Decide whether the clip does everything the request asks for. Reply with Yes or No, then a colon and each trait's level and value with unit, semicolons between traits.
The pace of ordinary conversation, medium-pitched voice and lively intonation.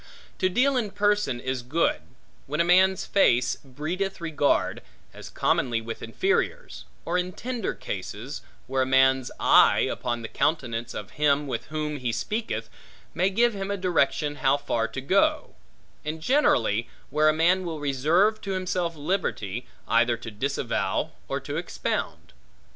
Yes: average, 155 wpm; medium, 155 Hz; wide, 6.5 semitones